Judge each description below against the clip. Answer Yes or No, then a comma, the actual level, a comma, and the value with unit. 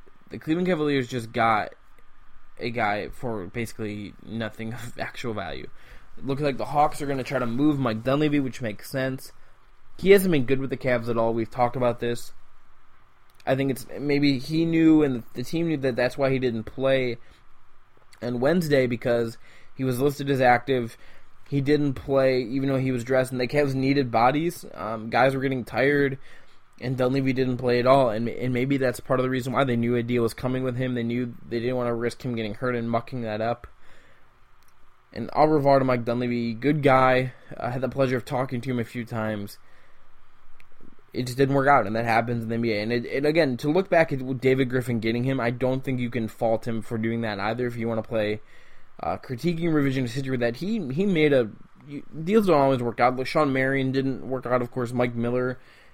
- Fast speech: Yes, fast, 220 wpm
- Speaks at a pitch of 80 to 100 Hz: No, low, 125 Hz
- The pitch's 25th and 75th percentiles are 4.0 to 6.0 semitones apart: No, narrow, 2.5 semitones